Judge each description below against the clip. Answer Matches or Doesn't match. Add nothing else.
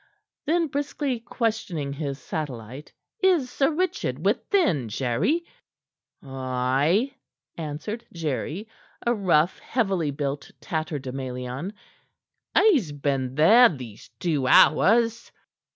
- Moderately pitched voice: Matches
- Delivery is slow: Matches